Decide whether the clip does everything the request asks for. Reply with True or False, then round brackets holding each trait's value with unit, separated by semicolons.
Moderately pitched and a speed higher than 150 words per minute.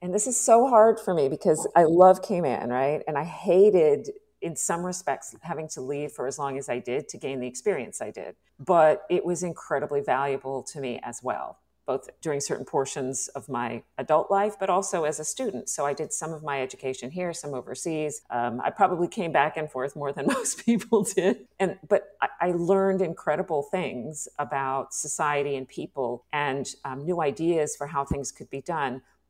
True (155 Hz; 200 wpm)